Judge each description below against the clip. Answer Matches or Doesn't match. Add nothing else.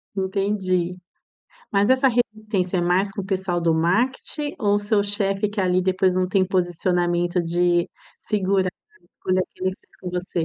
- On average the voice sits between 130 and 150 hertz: Doesn't match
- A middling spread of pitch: Doesn't match